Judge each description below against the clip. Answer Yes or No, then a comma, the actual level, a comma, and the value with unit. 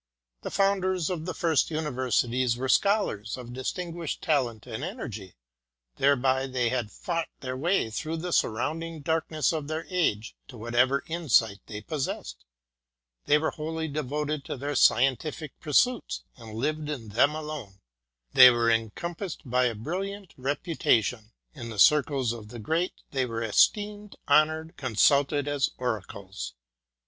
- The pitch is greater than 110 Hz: Yes, medium, 140 Hz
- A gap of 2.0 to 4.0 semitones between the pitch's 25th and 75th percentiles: No, average, 5.3 semitones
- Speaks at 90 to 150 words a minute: Yes, average, 140 wpm